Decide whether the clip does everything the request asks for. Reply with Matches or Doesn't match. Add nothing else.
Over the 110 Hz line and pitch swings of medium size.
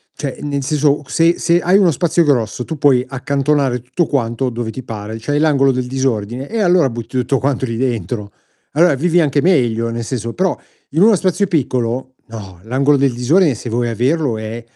Matches